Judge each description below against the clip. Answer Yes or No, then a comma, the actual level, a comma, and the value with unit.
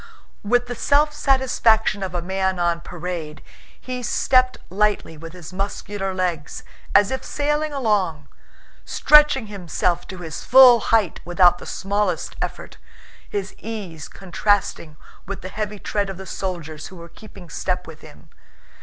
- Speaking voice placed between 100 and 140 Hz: No, high, 195 Hz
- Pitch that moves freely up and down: No, average, 4.3 semitones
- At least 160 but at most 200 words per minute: No, average, 145 wpm